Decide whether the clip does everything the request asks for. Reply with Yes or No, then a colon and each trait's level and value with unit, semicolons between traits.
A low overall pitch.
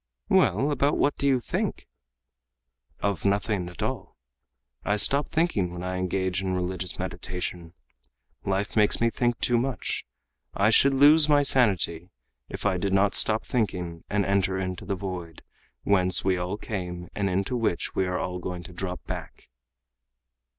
Yes: very low, 95 Hz